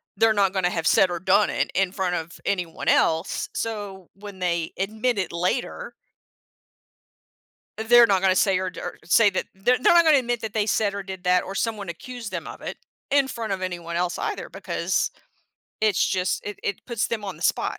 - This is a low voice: No, high, 195 Hz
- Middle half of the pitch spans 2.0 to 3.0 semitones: No, average, 3.4 semitones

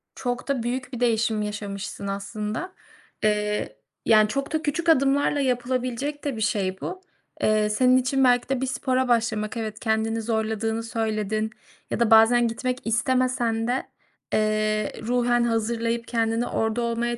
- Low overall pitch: No, high, 230 Hz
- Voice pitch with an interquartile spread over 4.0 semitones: No, average, 2.7 semitones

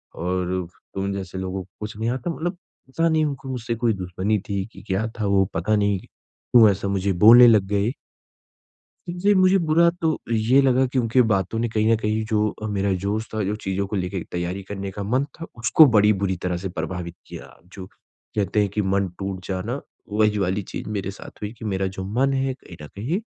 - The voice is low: Yes, low, 105 Hz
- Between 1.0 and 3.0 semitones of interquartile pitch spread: No, average, 3.6 semitones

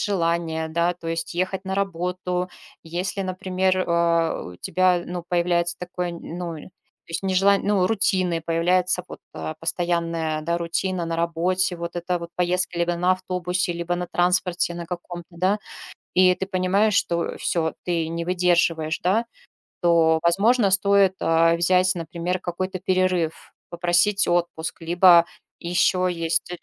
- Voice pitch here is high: No, medium, 175 Hz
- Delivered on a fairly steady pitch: Yes, narrow, 1.6 semitones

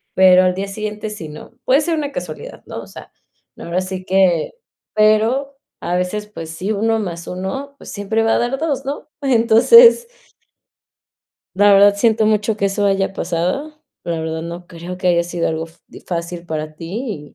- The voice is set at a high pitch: Yes, high, 195 Hz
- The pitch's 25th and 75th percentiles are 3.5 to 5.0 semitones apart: Yes, average, 4.5 semitones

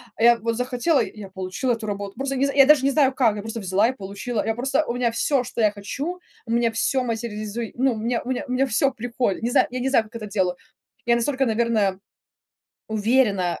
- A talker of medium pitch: No, high, 235 Hz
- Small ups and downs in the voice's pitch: No, average, 3.4 semitones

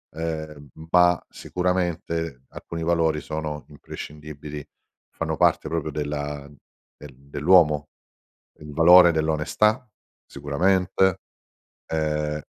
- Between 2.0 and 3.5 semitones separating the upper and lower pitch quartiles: Yes, average, 2.7 semitones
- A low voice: Yes, very low, 80 Hz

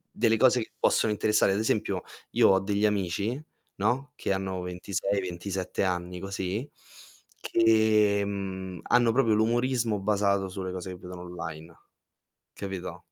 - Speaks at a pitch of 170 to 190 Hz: No, low, 100 Hz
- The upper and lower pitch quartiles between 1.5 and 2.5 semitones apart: No, average, 2.9 semitones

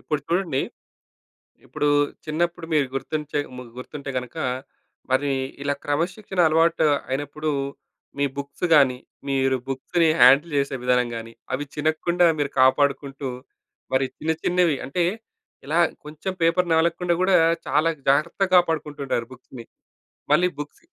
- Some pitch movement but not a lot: Yes, average, 3.6 semitones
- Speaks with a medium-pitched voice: Yes, medium, 150 Hz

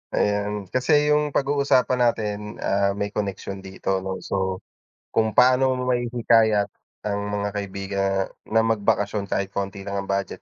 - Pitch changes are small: No, average, 3.6 semitones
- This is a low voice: Yes, low, 105 Hz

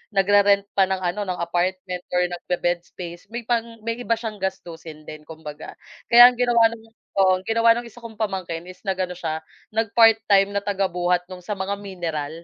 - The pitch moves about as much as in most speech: Yes, average, 4.0 semitones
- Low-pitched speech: No, high, 190 Hz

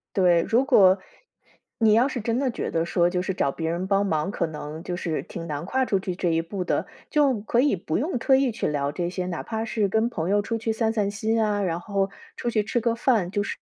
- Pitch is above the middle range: Yes, high, 200 Hz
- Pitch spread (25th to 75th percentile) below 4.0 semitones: No, average, 4.7 semitones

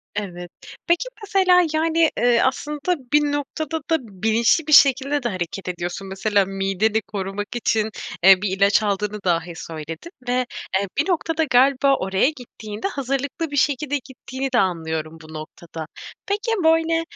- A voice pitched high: Yes, high, 235 Hz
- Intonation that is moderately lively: No, wide, 7.4 semitones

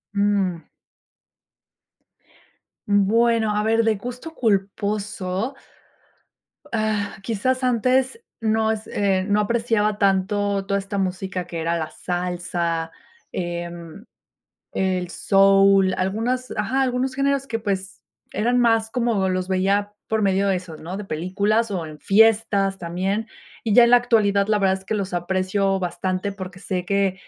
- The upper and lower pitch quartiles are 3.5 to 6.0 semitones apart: No, average, 2.9 semitones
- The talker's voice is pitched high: Yes, high, 200 Hz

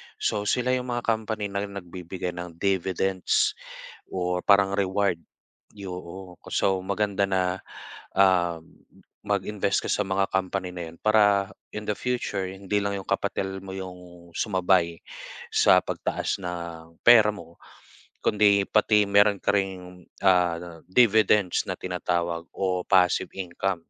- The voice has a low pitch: Yes, very low, 95 Hz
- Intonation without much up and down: Yes, narrow, 2.1 semitones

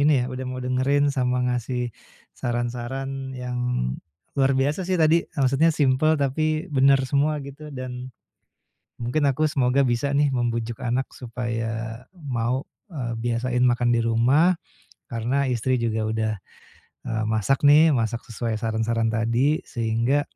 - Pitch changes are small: No, average, 3.1 semitones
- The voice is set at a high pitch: No, low, 125 Hz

